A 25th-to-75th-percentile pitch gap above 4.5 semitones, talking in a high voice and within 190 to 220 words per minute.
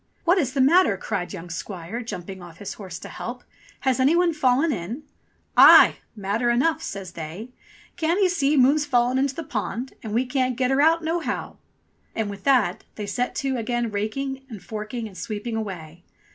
Yes: average, 5.2 semitones; high, 240 Hz; average, 195 wpm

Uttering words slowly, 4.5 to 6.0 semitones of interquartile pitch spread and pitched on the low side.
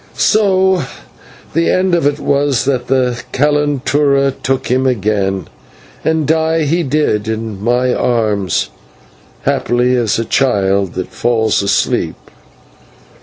Yes: slow, 120 wpm; average, 4.9 semitones; low, 130 Hz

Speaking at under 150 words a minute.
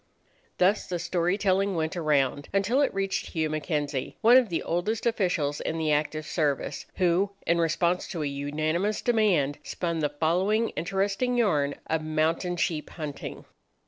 No: average, 155 wpm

